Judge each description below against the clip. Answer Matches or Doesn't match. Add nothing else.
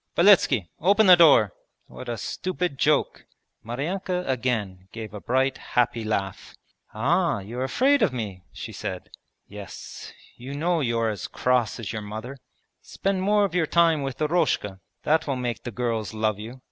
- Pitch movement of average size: Doesn't match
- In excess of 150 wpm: Matches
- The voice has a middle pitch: Doesn't match